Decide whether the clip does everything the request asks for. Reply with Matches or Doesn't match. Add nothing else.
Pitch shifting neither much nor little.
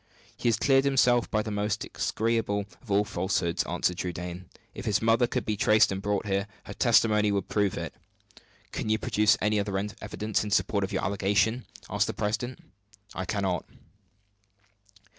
Doesn't match